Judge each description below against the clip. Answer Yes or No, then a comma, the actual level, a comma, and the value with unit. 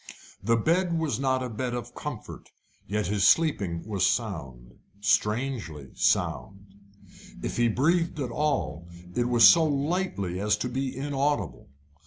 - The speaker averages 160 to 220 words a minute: No, average, 140 wpm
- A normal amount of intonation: No, wide, 6.0 semitones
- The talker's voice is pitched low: Yes, low, 120 Hz